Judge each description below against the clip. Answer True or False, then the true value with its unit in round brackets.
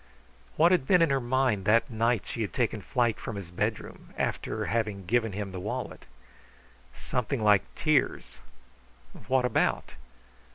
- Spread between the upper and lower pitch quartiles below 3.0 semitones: False (4.3 semitones)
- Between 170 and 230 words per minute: False (155 wpm)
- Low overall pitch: True (115 Hz)